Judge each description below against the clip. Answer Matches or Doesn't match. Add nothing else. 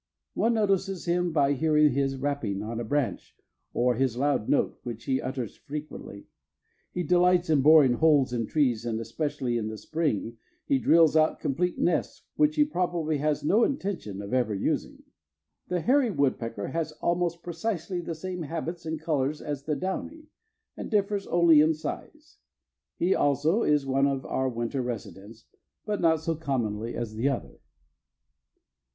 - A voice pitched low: Doesn't match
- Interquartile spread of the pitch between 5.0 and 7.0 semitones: Matches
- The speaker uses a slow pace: Doesn't match